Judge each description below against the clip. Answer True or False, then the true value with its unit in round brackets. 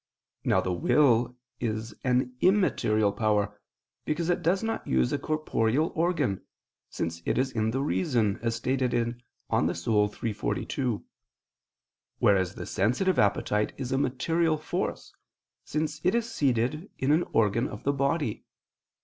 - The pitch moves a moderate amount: False (6.0 semitones)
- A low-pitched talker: True (125 Hz)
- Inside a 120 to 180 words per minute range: True (150 wpm)